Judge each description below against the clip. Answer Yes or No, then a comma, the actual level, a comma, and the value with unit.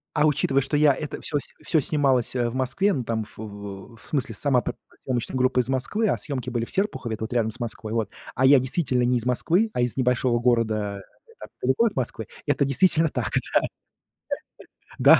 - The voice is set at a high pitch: No, low, 125 Hz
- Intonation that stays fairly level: No, average, 3.7 semitones